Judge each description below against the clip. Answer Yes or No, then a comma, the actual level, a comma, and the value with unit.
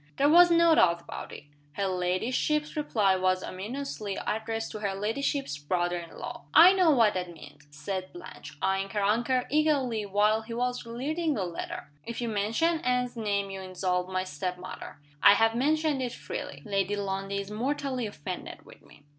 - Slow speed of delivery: No, average, 180 wpm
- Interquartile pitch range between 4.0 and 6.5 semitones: Yes, wide, 5.6 semitones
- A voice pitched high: Yes, high, 210 Hz